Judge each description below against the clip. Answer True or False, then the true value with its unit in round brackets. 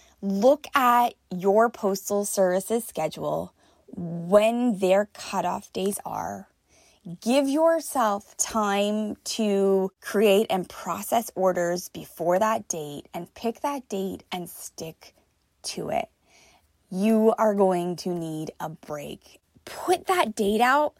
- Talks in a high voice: True (205 Hz)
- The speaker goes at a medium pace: False (115 wpm)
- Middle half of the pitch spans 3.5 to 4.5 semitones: True (4.1 semitones)